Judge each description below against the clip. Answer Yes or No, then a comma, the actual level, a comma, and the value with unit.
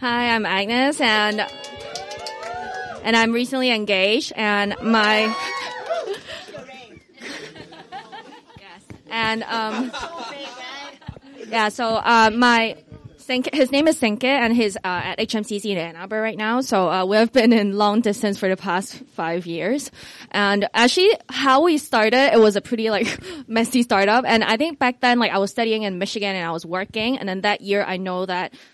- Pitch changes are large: No, average, 3.3 semitones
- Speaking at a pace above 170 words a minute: No, average, 160 wpm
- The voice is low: No, high, 220 Hz